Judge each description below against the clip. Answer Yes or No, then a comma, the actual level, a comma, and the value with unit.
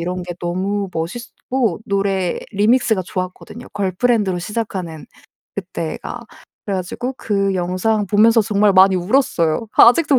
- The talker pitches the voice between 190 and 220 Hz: Yes, high, 200 Hz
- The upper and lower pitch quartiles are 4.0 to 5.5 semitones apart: No, average, 3.6 semitones